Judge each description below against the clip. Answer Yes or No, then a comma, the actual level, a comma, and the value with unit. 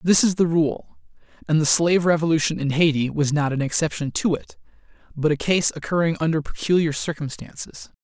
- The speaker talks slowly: No, average, 170 wpm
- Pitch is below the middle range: No, medium, 160 Hz